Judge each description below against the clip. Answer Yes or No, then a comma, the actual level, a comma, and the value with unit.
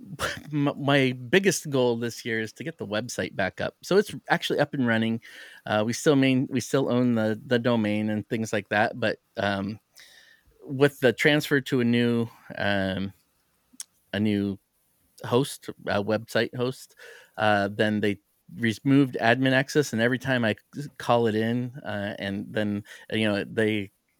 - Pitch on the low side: Yes, low, 115 Hz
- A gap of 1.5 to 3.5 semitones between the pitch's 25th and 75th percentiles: No, average, 3.9 semitones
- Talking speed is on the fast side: No, average, 165 wpm